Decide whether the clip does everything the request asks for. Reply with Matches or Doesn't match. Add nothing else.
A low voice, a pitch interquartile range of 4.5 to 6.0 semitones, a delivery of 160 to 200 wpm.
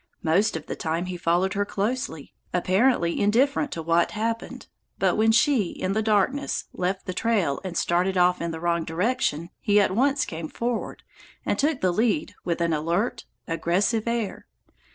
Doesn't match